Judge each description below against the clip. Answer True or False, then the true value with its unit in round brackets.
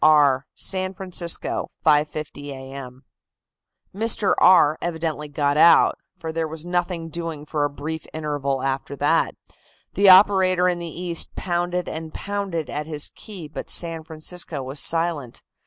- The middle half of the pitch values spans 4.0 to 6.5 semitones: False (3.2 semitones)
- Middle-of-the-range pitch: True (160 Hz)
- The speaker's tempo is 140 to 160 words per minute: True (145 wpm)